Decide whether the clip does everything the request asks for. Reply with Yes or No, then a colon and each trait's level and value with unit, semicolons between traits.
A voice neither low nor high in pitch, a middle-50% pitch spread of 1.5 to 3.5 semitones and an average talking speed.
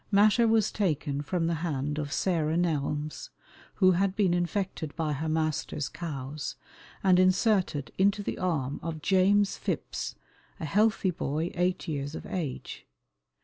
No: medium, 170 Hz; average, 4.2 semitones; average, 145 wpm